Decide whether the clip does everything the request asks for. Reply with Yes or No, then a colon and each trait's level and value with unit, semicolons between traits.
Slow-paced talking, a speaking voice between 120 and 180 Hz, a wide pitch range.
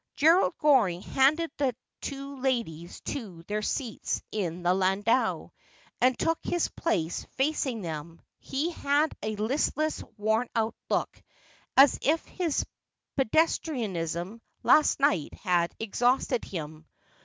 No: slow, 120 wpm; high, 235 Hz; wide, 7.5 semitones